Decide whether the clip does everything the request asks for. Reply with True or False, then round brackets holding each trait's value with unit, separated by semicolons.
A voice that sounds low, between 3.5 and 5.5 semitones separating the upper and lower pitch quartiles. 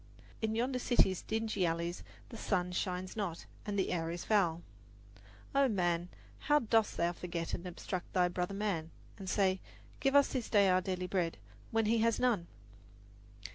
False (190 Hz; 4.0 semitones)